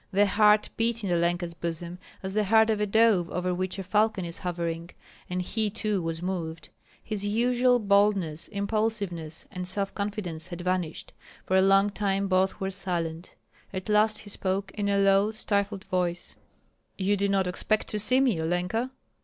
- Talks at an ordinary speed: Yes, average, 175 wpm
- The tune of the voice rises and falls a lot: No, average, 2.9 semitones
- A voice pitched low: No, high, 195 Hz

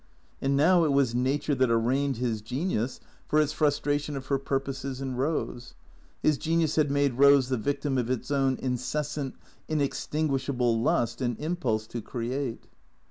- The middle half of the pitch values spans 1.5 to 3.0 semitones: Yes, narrow, 2.6 semitones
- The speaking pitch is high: No, low, 135 Hz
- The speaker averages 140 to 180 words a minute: Yes, average, 160 wpm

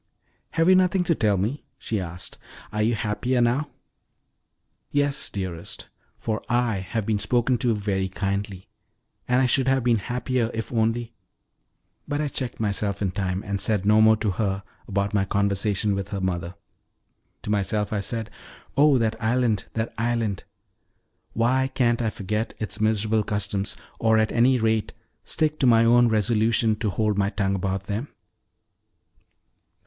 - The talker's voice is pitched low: Yes, low, 110 Hz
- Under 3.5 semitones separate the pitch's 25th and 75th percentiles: Yes, average, 3.1 semitones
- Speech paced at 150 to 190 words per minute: Yes, average, 160 wpm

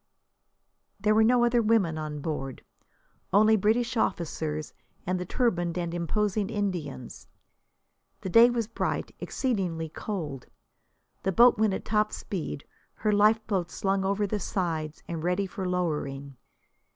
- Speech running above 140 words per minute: No, slow, 135 wpm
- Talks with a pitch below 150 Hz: No, high, 190 Hz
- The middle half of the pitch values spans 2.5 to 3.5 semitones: No, average, 4.5 semitones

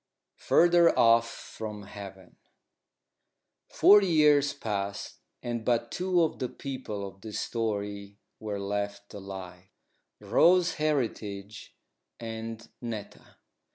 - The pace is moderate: No, slow, 100 wpm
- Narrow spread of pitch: No, average, 5.2 semitones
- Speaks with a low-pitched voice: Yes, low, 110 Hz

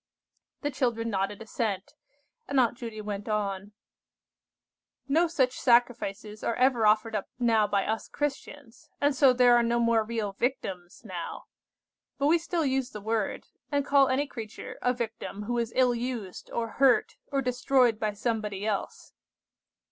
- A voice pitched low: No, high, 235 Hz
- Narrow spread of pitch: No, average, 3.5 semitones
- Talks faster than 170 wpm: No, average, 155 wpm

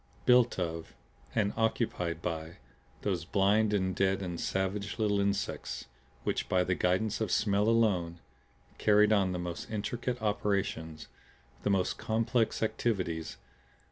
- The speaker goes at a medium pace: No, slow, 130 wpm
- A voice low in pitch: Yes, low, 100 Hz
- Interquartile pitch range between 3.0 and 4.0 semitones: Yes, average, 3.4 semitones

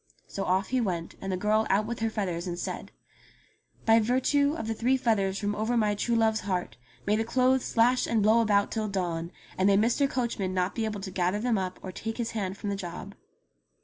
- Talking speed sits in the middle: No, fast, 230 wpm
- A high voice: Yes, high, 210 Hz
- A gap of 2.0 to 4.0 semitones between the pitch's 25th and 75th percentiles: Yes, average, 3.2 semitones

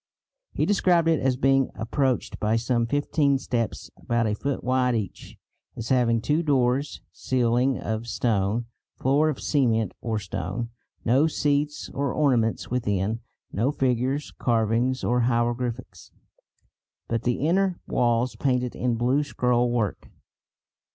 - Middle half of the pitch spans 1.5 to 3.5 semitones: Yes, average, 2.9 semitones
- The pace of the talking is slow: Yes, slow, 130 wpm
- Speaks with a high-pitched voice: No, low, 125 Hz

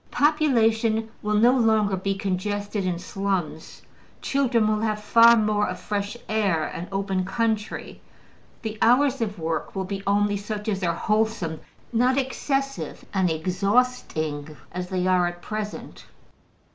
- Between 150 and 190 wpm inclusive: No, average, 140 wpm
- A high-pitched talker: Yes, high, 210 Hz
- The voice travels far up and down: No, average, 3.3 semitones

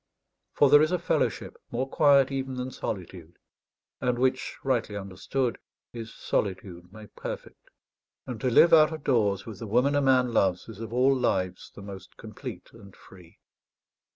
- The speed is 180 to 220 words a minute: No, average, 165 wpm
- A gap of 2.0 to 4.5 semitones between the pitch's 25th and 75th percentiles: No, average, 5.2 semitones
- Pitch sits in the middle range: No, low, 120 Hz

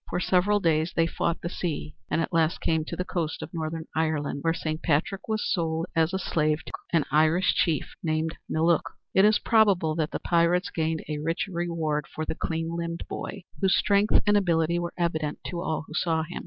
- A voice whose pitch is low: No, medium, 165 Hz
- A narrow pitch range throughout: Yes, narrow, 2.0 semitones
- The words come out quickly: Yes, fast, 210 wpm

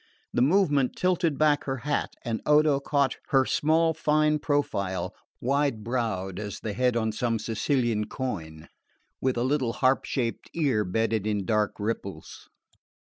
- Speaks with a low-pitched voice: Yes, low, 125 Hz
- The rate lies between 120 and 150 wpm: Yes, average, 145 wpm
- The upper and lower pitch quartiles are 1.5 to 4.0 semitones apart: No, average, 5.1 semitones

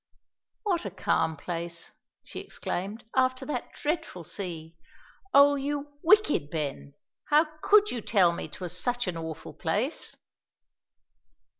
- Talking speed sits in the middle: No, slow, 125 wpm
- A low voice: No, high, 205 Hz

